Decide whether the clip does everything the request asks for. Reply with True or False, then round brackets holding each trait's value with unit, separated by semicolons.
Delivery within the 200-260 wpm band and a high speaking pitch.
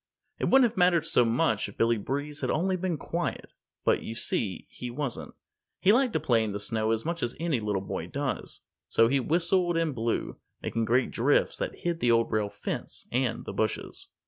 False (205 wpm; 125 Hz)